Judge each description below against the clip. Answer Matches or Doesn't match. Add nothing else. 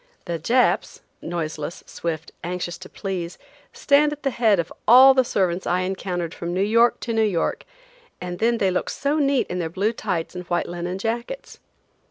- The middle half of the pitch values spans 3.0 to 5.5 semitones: Matches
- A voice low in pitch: Doesn't match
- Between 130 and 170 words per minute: Doesn't match